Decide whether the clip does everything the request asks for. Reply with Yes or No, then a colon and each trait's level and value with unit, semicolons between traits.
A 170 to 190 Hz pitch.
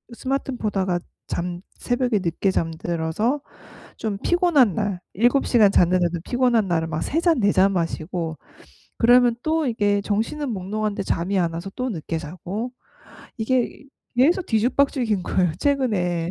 No: high, 205 Hz